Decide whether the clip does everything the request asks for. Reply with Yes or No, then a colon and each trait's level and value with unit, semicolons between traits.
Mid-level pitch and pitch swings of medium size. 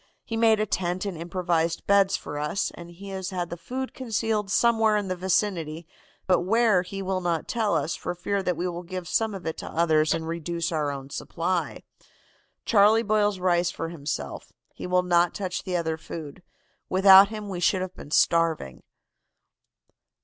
Yes: medium, 180 Hz; average, 3.1 semitones